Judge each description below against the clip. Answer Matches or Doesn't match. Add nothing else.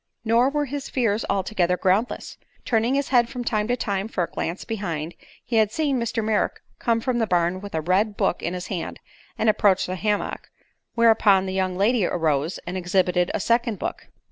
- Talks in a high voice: Matches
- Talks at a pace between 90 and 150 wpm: Doesn't match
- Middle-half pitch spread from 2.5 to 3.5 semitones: Doesn't match